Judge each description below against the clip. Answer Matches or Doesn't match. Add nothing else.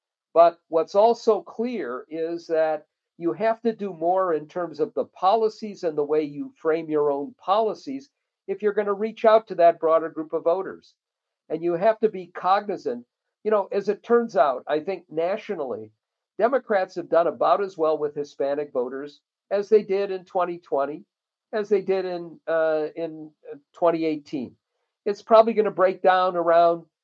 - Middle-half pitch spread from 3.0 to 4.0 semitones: Doesn't match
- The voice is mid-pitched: Matches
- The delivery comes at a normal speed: Matches